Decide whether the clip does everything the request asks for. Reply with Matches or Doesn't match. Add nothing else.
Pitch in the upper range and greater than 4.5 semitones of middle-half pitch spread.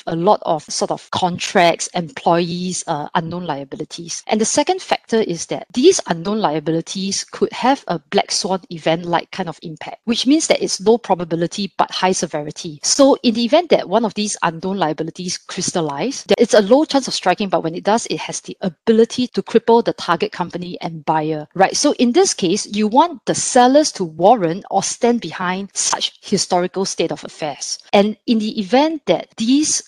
Matches